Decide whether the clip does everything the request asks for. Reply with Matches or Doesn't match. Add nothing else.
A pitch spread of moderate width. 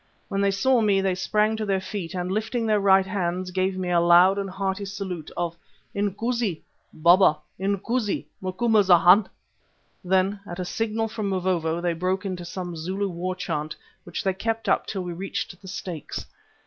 Doesn't match